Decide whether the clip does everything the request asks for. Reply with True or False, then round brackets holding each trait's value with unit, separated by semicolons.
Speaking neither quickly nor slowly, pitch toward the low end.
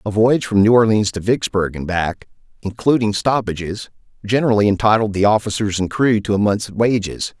True (170 wpm; 105 Hz)